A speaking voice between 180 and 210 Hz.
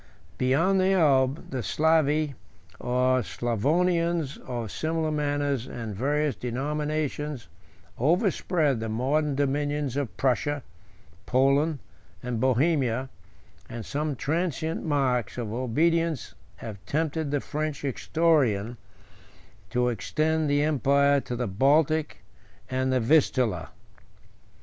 No: medium, 140 Hz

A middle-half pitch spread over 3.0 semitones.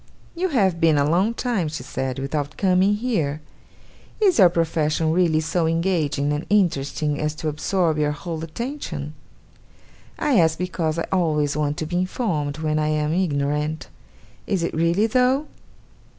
Yes: average, 3.8 semitones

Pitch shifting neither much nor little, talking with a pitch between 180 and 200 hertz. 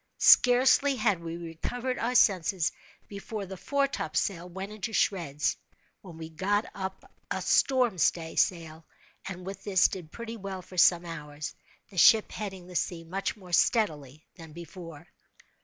Yes: average, 4.1 semitones; medium, 185 Hz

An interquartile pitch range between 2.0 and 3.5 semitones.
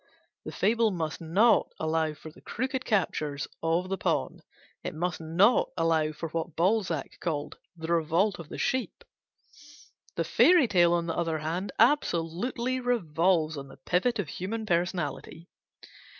No: average, 4.6 semitones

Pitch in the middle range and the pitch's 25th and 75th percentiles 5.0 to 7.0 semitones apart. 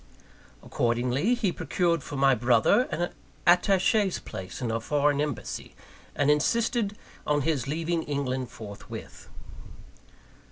Yes: medium, 145 Hz; wide, 5.6 semitones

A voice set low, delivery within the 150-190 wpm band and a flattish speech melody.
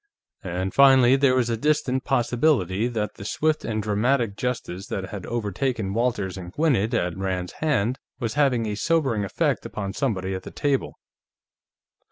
No: low, 115 Hz; average, 160 wpm; average, 5.2 semitones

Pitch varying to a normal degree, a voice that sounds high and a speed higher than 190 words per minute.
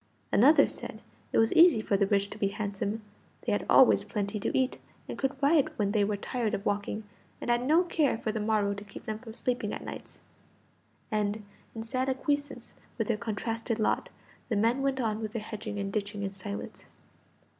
Yes: average, 3.5 semitones; high, 220 Hz; average, 200 wpm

